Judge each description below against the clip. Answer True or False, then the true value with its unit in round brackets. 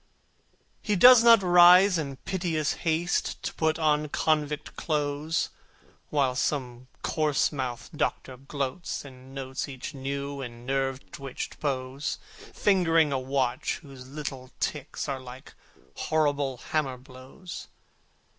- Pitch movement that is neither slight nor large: True (3.2 semitones)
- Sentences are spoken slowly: True (120 wpm)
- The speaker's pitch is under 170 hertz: True (140 Hz)